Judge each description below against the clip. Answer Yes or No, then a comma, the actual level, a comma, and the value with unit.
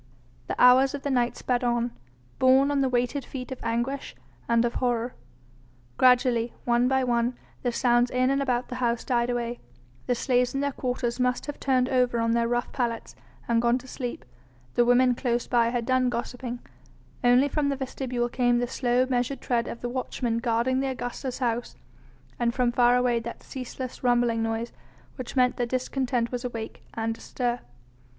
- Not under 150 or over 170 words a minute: No, average, 185 wpm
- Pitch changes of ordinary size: No, narrow, 1.3 semitones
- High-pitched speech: Yes, high, 245 Hz